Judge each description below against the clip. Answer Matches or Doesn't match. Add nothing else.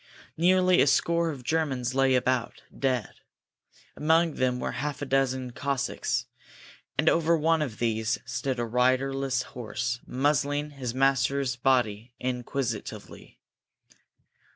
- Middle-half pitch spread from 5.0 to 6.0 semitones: Doesn't match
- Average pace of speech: Doesn't match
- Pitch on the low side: Matches